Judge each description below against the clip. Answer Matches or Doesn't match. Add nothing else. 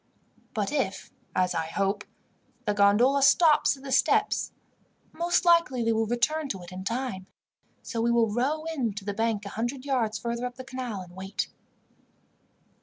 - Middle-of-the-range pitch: Doesn't match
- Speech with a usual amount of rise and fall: Matches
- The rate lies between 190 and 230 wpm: Doesn't match